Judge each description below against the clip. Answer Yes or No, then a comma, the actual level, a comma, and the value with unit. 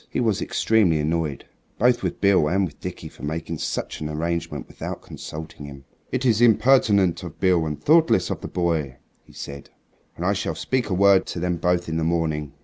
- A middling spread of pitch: Yes, average, 4.3 semitones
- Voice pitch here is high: No, very low, 85 Hz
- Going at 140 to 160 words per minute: No, average, 200 wpm